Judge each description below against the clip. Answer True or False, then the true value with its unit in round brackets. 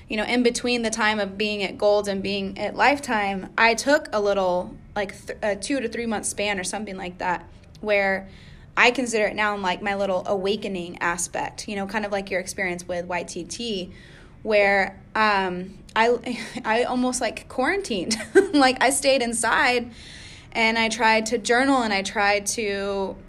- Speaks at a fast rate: False (180 wpm)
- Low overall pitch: False (210 Hz)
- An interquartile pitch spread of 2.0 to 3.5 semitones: True (3.2 semitones)